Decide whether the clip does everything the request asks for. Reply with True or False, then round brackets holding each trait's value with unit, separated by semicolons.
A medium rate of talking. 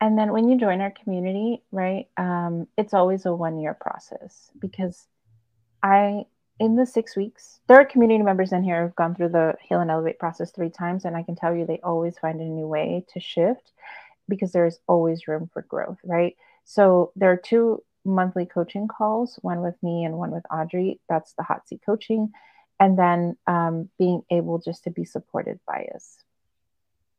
True (190 wpm)